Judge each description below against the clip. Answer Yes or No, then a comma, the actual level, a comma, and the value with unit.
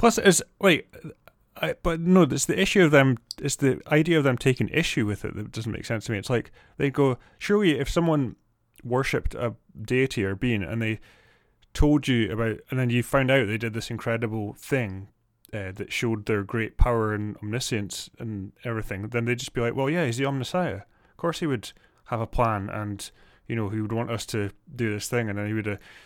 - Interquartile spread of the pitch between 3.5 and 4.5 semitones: Yes, average, 4.2 semitones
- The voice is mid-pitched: No, low, 115 Hz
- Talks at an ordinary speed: No, fast, 220 wpm